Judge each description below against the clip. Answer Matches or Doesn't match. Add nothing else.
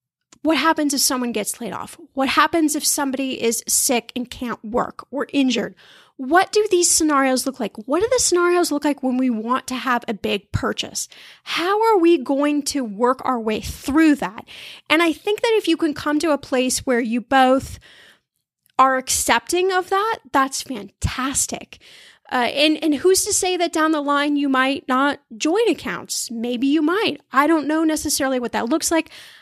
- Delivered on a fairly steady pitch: Doesn't match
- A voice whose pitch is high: Matches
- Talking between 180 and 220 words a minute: Matches